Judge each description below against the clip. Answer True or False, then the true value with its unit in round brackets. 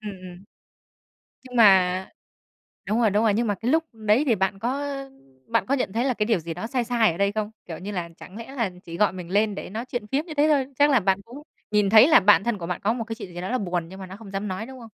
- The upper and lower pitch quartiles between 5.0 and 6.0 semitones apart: False (4.1 semitones)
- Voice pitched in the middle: False (215 Hz)